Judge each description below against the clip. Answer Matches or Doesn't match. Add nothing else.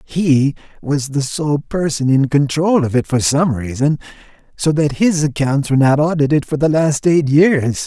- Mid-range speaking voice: Matches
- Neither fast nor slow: Matches